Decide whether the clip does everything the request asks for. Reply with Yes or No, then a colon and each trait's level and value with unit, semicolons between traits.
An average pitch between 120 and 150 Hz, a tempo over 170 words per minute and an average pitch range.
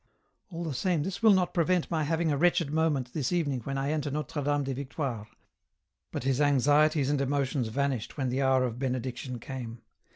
Yes: medium, 140 Hz; average, 200 wpm; average, 3.2 semitones